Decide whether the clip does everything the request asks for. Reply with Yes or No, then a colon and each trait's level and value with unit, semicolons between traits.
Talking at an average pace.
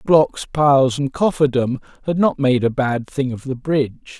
Yes: average, 185 wpm